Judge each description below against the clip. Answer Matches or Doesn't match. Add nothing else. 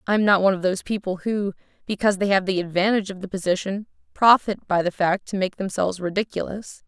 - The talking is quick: Matches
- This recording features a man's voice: Doesn't match